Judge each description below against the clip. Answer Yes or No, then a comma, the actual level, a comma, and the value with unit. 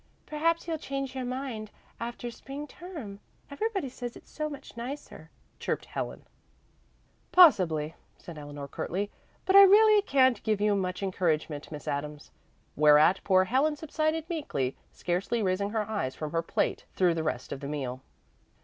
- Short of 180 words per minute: Yes, average, 155 wpm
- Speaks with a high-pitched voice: Yes, high, 215 Hz